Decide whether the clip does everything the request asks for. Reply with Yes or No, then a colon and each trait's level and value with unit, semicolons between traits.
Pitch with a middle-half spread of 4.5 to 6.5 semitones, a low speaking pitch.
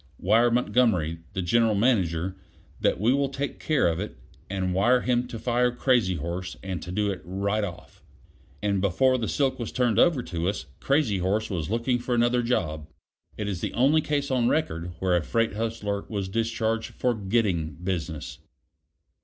Yes: average, 4.8 semitones; low, 110 Hz